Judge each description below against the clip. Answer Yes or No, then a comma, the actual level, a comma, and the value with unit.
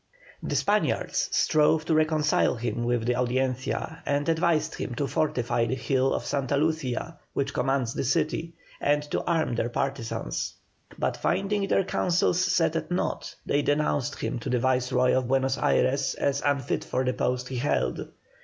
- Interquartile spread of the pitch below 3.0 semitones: No, average, 3.7 semitones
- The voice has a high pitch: No, medium, 140 Hz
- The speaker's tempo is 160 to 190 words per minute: Yes, average, 165 wpm